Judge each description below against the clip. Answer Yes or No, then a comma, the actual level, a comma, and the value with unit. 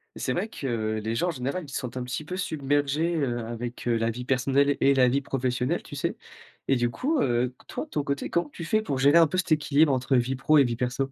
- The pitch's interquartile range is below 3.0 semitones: No, average, 3.4 semitones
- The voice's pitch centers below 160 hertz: Yes, low, 135 Hz